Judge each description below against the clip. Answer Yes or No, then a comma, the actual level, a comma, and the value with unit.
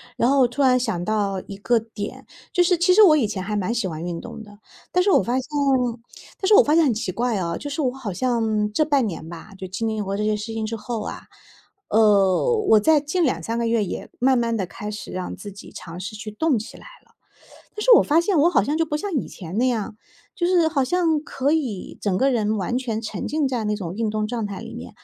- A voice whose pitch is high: Yes, high, 230 Hz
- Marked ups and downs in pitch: Yes, wide, 5.7 semitones